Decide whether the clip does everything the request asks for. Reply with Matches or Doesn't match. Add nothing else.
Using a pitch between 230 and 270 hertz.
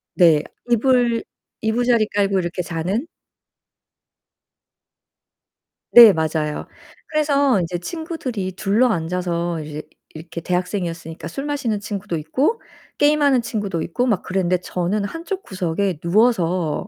Doesn't match